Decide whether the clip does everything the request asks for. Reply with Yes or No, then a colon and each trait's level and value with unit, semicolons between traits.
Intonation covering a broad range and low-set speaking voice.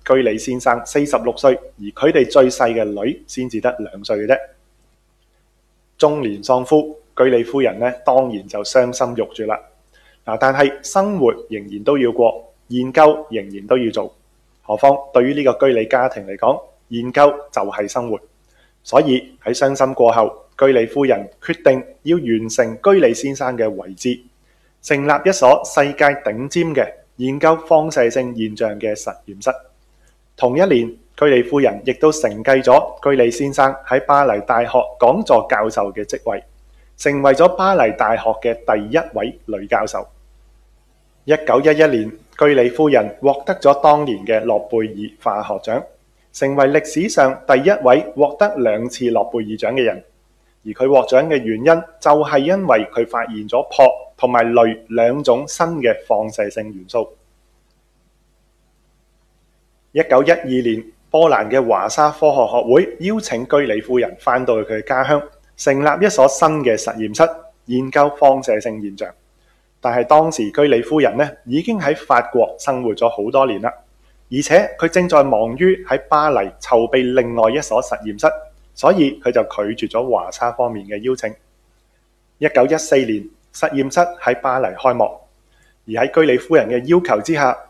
No: average, 4.3 semitones; low, 130 Hz